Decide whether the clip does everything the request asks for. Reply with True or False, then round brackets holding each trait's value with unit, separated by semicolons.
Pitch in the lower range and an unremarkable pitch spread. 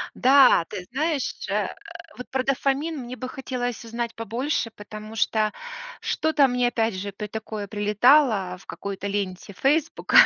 False (235 Hz; 4.4 semitones)